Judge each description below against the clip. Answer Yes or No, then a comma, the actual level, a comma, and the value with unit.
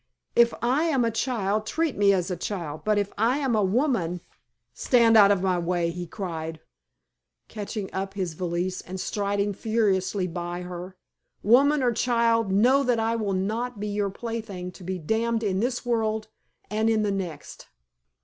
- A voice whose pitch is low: No, high, 205 Hz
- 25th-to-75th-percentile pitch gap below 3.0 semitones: No, average, 3.8 semitones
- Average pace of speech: Yes, average, 180 wpm